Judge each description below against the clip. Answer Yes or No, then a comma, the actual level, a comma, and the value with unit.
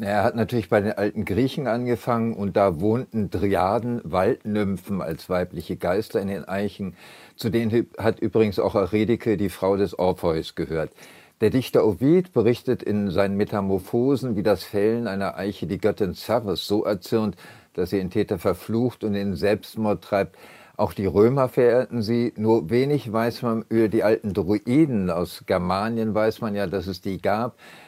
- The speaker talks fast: No, average, 170 wpm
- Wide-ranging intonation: No, average, 2.7 semitones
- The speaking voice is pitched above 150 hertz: No, low, 110 Hz